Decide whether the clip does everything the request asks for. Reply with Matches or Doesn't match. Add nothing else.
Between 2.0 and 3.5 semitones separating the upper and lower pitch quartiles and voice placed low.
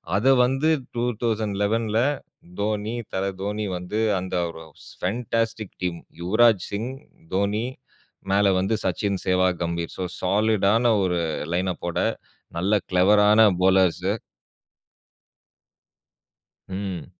Matches